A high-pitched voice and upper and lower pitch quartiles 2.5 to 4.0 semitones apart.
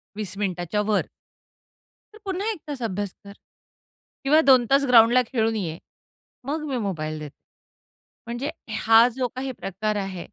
No: high, 225 Hz; average, 5.2 semitones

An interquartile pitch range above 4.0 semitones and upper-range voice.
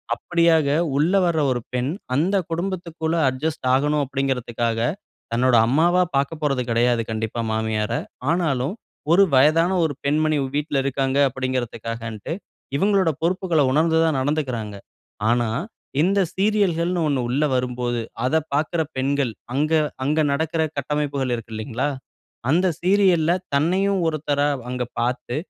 No: average, 4.6 semitones; medium, 145 Hz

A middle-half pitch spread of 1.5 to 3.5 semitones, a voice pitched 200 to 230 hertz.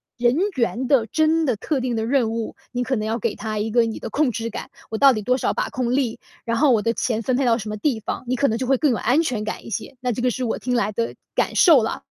No: narrow, 2.5 semitones; high, 240 Hz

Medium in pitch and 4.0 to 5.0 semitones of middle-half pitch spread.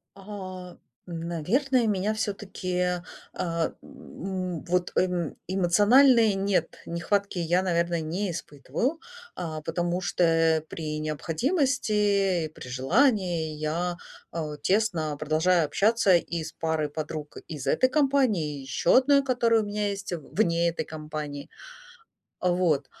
Yes: medium, 175 Hz; average, 4.4 semitones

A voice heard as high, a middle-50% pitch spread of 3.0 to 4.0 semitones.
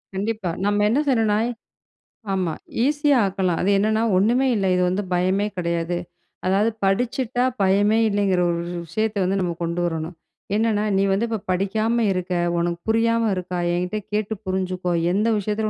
Yes: high, 195 Hz; average, 3.3 semitones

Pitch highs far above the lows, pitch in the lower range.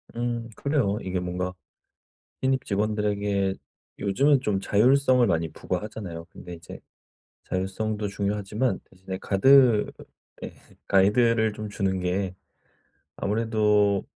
No: average, 3.1 semitones; low, 105 Hz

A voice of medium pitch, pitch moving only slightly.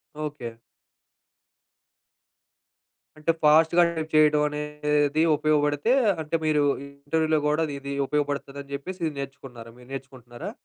Yes: medium, 150 Hz; narrow, 1.6 semitones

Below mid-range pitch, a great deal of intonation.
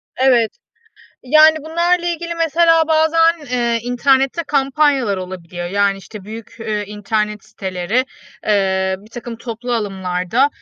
No: high, 235 Hz; wide, 7.3 semitones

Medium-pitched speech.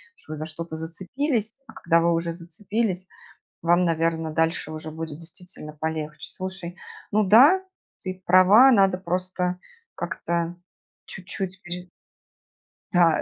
Yes: medium, 175 Hz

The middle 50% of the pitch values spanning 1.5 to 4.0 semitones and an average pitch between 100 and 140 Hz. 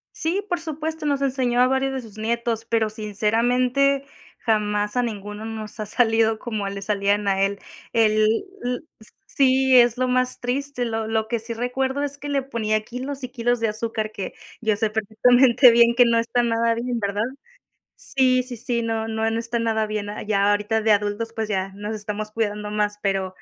No: average, 2.8 semitones; high, 230 Hz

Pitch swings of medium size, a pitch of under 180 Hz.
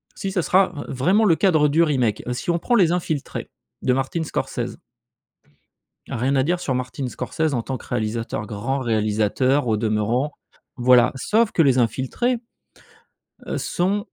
No: wide, 6.0 semitones; low, 135 Hz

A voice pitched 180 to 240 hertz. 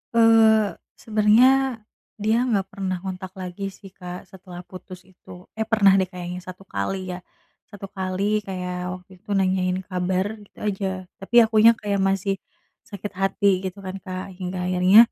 Yes: high, 190 Hz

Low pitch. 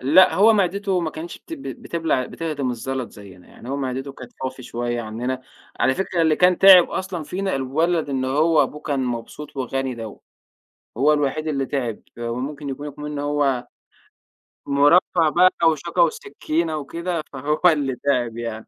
No: medium, 145 Hz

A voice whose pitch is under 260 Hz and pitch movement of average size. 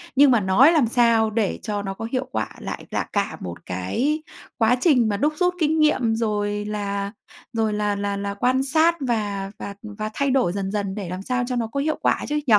Yes: high, 220 Hz; average, 4.5 semitones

